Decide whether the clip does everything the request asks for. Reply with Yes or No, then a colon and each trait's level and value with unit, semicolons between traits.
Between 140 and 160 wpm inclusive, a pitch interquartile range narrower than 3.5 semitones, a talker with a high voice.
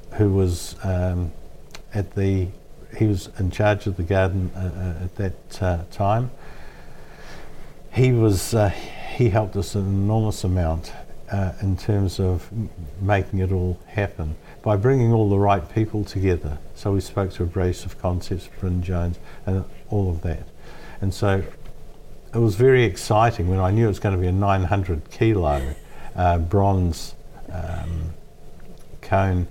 No: average, 155 wpm; narrow, 2.6 semitones; very low, 95 Hz